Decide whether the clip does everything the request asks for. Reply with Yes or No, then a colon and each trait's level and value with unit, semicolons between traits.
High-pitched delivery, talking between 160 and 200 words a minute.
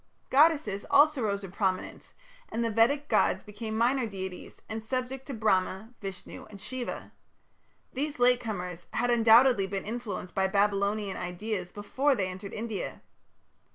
No: high, 215 Hz; average, 145 wpm